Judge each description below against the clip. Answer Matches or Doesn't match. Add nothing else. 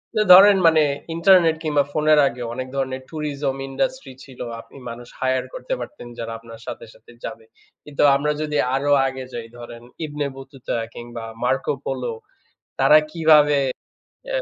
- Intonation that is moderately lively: Matches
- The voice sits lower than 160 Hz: Matches